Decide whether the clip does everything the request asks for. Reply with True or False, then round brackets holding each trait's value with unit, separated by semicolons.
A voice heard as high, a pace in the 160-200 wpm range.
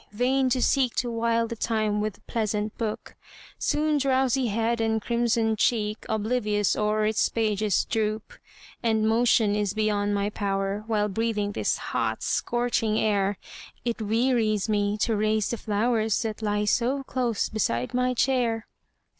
False (220 Hz; 145 wpm)